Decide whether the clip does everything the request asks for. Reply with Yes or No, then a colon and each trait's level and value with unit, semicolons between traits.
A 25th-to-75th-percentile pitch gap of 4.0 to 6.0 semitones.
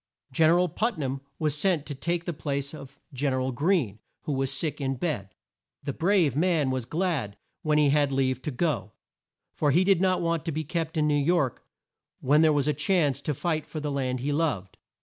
No: average, 3.5 semitones